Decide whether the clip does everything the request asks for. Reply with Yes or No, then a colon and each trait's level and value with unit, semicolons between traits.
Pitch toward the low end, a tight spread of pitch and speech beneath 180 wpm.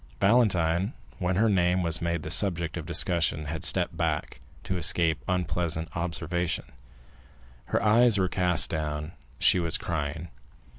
Yes: very low, 85 Hz; narrow, 2.3 semitones; average, 145 wpm